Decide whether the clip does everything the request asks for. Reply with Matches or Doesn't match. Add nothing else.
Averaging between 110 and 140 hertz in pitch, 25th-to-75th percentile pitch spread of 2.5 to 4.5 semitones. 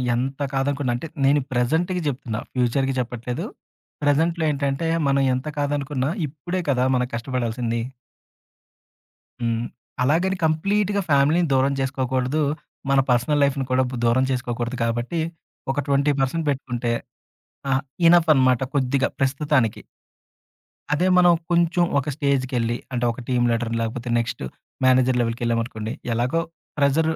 Matches